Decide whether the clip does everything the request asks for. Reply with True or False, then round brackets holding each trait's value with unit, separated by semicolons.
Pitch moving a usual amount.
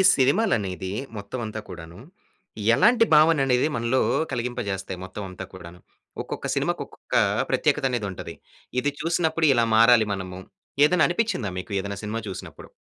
False (7.2 semitones)